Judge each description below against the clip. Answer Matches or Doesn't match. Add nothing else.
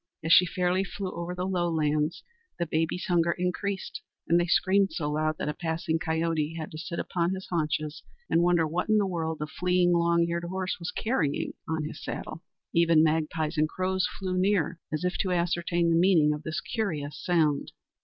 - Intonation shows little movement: Matches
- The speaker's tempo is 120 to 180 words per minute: Doesn't match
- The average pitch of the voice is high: Doesn't match